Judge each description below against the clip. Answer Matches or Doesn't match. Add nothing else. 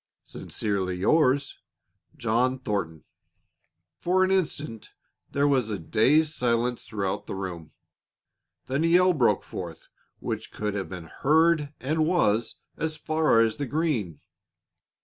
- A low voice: Matches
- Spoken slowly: Matches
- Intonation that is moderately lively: Doesn't match